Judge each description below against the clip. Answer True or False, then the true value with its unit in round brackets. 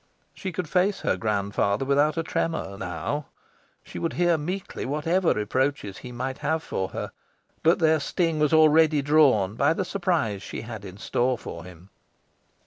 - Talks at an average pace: True (165 wpm)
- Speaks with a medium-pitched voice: True (145 Hz)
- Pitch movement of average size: False (7.5 semitones)